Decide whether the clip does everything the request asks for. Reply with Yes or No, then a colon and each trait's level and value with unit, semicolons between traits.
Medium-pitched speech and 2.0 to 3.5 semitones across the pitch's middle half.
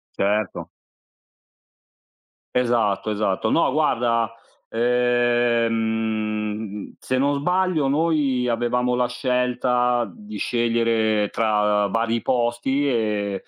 No: low, 120 Hz; narrow, 2.4 semitones